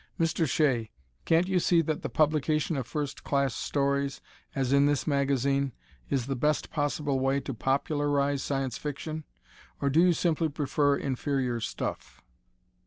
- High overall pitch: No, medium, 140 Hz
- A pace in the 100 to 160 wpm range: Yes, average, 150 wpm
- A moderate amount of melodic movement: No, narrow, 2.1 semitones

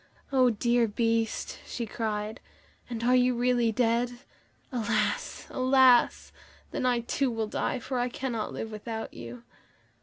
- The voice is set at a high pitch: Yes, high, 235 Hz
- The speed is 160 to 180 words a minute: No, average, 140 wpm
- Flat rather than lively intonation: Yes, narrow, 2.0 semitones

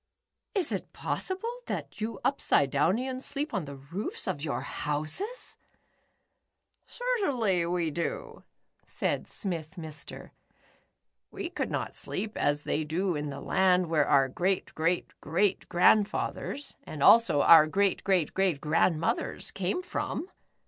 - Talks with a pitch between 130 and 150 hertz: No, medium, 180 Hz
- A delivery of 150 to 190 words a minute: No, slow, 135 wpm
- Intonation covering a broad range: Yes, wide, 6.1 semitones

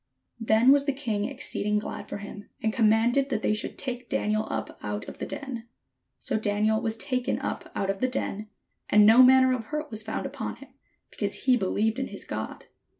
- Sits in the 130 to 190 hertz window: No, high, 225 Hz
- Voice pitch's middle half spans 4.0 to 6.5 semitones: No, average, 3.4 semitones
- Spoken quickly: Yes, fast, 210 wpm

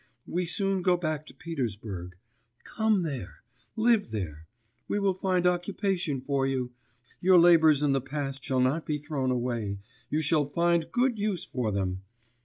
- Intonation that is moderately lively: No, wide, 5.9 semitones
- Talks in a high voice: No, medium, 150 Hz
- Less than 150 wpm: No, average, 160 wpm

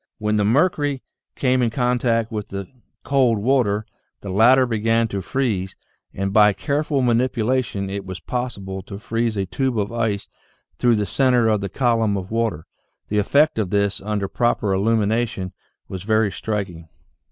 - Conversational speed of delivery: Yes, average, 160 wpm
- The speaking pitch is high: No, low, 110 Hz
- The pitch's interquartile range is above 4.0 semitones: No, average, 3.6 semitones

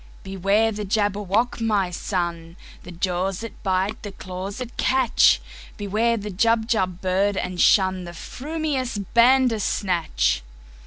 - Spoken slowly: Yes, slow, 105 wpm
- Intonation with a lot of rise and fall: No, average, 3.6 semitones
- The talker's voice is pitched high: Yes, high, 200 Hz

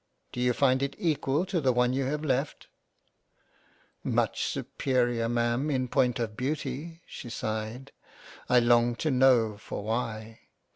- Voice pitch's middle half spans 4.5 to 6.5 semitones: No, narrow, 2.6 semitones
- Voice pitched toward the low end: Yes, low, 125 Hz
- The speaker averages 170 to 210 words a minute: No, average, 155 wpm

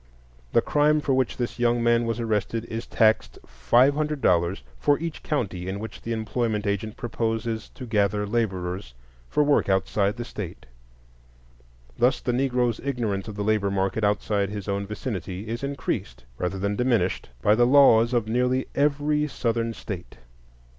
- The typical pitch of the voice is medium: No, low, 115 Hz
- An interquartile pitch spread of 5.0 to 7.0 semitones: No, average, 3.7 semitones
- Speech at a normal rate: Yes, average, 160 wpm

